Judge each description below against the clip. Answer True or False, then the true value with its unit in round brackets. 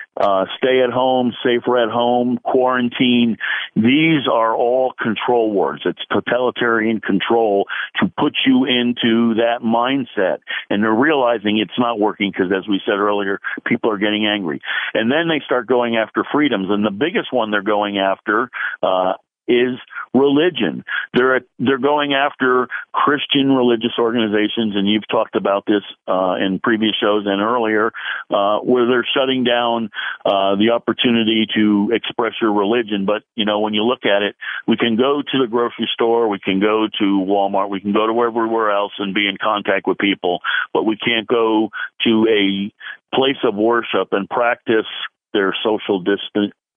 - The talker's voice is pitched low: True (115 Hz)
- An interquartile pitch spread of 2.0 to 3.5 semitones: True (3.0 semitones)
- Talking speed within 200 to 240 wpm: False (170 wpm)